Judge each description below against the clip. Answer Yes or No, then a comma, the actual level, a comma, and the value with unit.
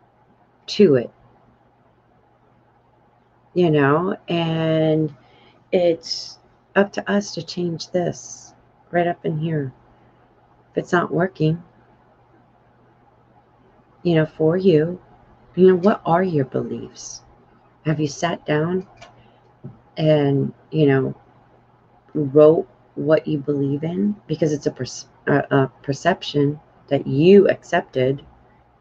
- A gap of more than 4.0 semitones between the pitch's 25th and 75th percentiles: Yes, average, 4.9 semitones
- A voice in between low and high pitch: Yes, medium, 155 Hz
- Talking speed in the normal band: No, slow, 110 wpm